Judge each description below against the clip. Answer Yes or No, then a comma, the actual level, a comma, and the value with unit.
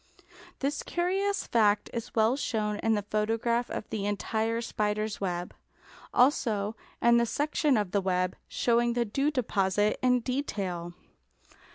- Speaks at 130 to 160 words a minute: Yes, average, 140 wpm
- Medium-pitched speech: No, high, 225 Hz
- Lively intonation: No, average, 3.1 semitones